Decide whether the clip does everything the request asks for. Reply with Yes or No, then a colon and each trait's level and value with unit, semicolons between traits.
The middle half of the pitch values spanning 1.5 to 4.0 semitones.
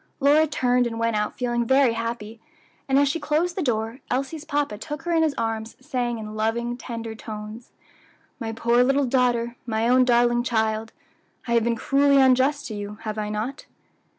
Yes: average, 3.4 semitones